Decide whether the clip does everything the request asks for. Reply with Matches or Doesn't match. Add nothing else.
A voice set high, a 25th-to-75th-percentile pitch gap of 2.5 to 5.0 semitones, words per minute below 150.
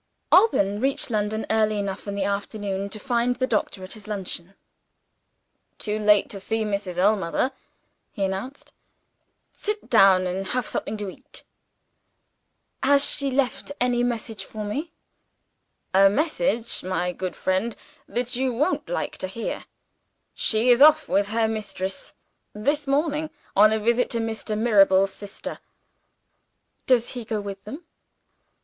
Matches